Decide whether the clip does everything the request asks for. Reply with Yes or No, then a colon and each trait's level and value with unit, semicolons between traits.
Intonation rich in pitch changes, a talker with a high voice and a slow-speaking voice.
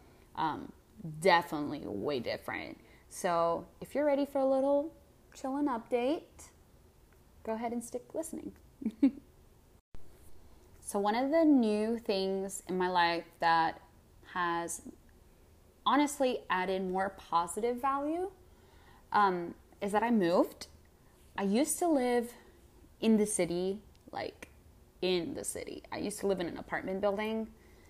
Yes: wide, 6.8 semitones; high, 210 Hz; slow, 125 wpm